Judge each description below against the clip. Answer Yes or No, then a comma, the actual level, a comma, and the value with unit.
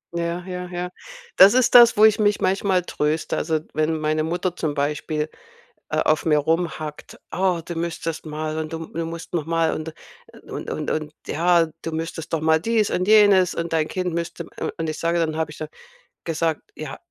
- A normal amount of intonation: No, narrow, 2.3 semitones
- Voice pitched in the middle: Yes, medium, 165 Hz